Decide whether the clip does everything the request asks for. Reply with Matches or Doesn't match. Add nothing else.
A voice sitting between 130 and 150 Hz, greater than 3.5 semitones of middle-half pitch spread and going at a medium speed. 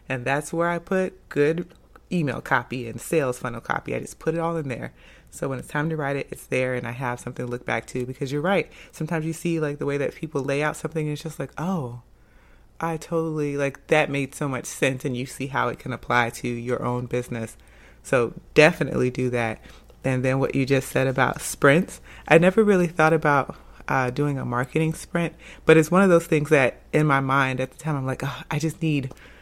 Doesn't match